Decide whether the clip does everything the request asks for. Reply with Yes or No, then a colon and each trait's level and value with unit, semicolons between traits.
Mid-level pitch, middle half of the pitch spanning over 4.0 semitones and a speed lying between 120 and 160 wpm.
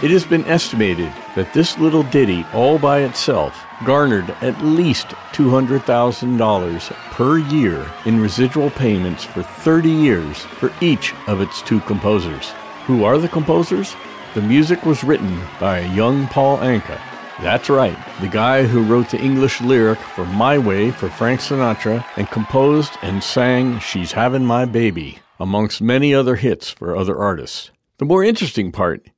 No: low, 125 Hz; average, 5.3 semitones; average, 155 wpm